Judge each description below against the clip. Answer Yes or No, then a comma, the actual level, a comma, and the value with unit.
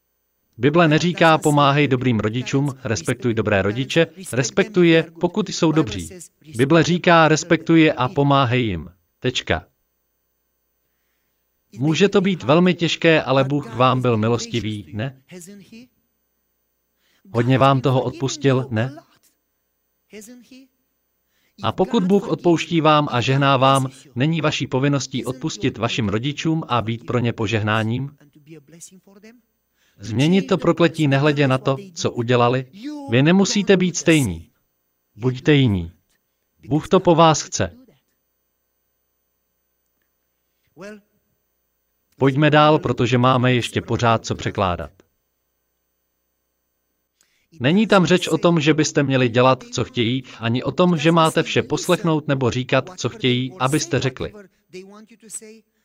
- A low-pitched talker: Yes, low, 130 Hz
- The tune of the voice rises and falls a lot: Yes, wide, 7.5 semitones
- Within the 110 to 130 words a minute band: Yes, average, 115 wpm